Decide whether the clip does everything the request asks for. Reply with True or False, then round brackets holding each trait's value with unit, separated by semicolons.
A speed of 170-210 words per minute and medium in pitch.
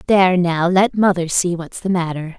True (200 wpm; 180 Hz)